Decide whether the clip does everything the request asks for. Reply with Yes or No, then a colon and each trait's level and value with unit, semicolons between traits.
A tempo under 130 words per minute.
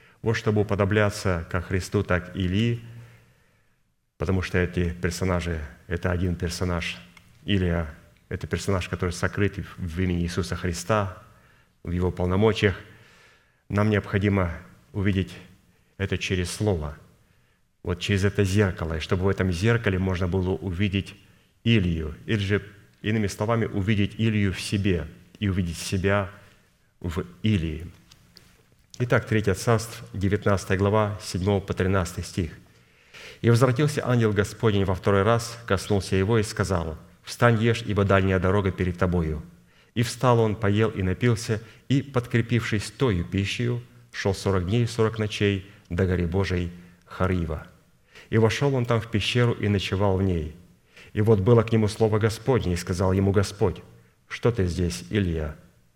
No: average, 140 wpm